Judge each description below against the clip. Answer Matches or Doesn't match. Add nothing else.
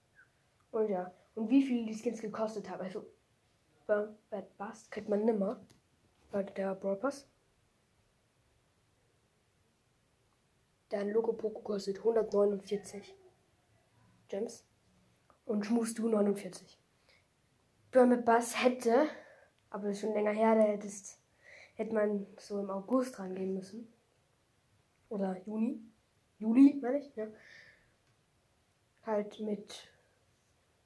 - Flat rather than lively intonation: Doesn't match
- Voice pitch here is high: Matches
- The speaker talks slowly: Matches